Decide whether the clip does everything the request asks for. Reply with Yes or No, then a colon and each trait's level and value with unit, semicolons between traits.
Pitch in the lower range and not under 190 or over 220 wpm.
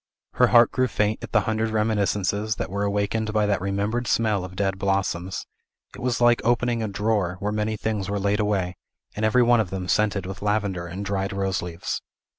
Yes: low, 105 Hz; fast, 205 wpm